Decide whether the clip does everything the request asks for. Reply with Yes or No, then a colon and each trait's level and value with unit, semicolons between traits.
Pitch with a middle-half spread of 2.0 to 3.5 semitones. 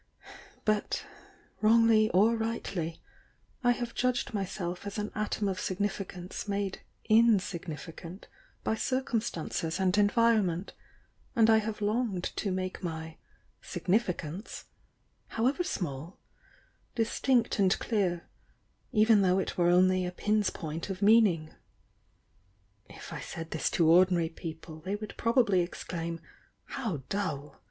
No: average, 4.1 semitones